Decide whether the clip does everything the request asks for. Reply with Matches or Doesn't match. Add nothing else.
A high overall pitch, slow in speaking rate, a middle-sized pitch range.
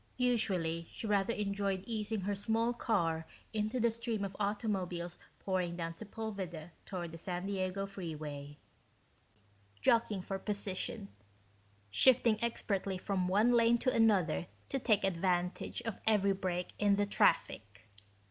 Matches